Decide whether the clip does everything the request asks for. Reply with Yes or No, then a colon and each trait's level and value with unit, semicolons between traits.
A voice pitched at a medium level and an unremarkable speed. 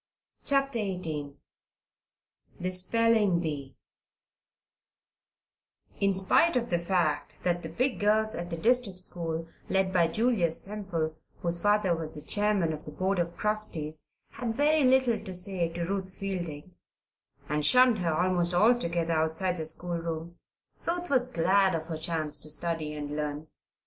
Yes: medium, 180 Hz; average, 150 wpm